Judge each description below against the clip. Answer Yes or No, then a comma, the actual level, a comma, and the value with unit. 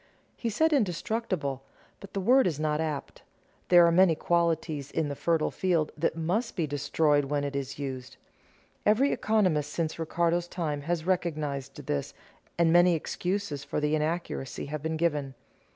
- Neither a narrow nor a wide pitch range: Yes, average, 3.3 semitones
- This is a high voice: No, medium, 160 Hz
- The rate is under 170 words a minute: Yes, average, 160 wpm